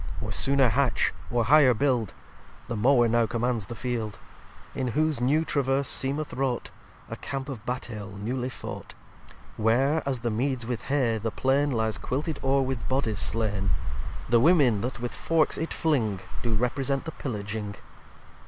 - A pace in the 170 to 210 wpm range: No, average, 160 wpm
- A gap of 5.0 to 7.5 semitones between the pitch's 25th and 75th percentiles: No, average, 3.3 semitones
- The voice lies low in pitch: Yes, low, 125 Hz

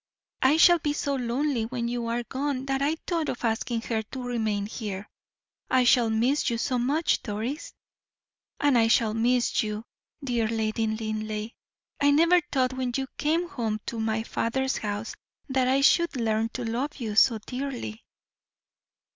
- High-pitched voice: Yes, high, 240 Hz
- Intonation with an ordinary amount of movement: Yes, average, 3.5 semitones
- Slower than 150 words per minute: No, average, 165 wpm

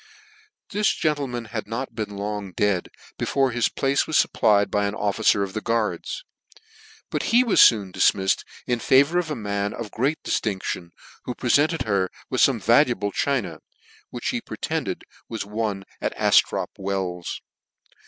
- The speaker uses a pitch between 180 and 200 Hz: No, low, 110 Hz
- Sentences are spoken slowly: No, average, 155 wpm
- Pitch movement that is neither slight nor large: Yes, average, 4.7 semitones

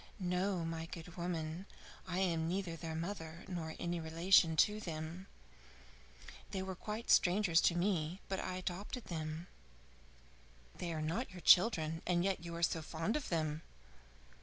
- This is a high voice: No, medium, 175 Hz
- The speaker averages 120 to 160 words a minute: Yes, average, 155 wpm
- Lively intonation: No, narrow, 2.6 semitones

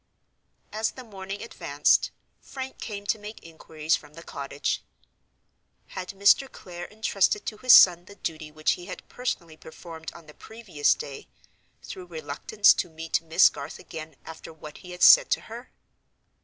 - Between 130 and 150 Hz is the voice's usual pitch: No, medium, 175 Hz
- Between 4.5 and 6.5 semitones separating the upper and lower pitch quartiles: Yes, average, 4.8 semitones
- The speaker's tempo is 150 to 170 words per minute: Yes, average, 160 wpm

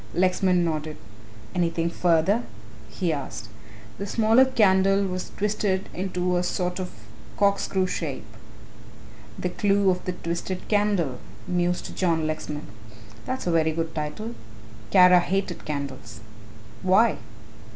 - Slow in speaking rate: Yes, slow, 120 wpm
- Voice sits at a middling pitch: Yes, medium, 180 Hz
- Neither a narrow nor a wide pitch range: Yes, average, 3.0 semitones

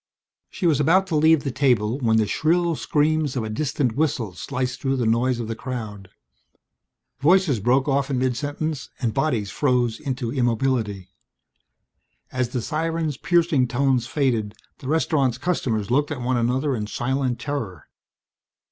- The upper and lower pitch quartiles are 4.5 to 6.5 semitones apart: No, average, 3.9 semitones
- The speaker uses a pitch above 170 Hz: No, low, 130 Hz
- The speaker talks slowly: No, average, 155 wpm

